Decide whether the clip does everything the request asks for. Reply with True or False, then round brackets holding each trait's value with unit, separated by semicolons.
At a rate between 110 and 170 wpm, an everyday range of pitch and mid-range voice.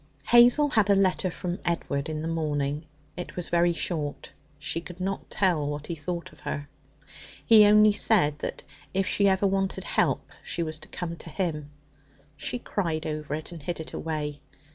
False (185 wpm; 4.0 semitones; 170 Hz)